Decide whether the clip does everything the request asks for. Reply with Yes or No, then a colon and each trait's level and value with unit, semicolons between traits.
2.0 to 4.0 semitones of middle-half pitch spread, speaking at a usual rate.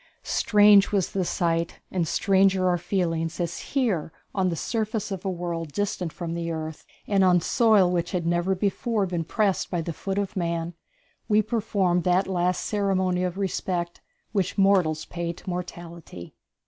Yes: narrow, 2.5 semitones; average, 165 wpm